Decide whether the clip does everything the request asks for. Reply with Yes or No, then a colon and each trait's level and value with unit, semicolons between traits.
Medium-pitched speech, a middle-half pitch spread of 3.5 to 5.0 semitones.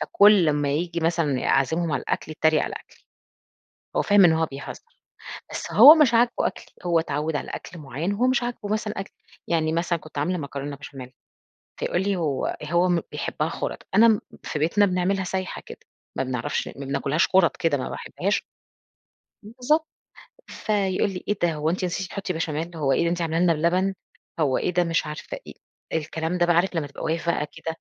Yes: medium, 170 Hz; average, 3.9 semitones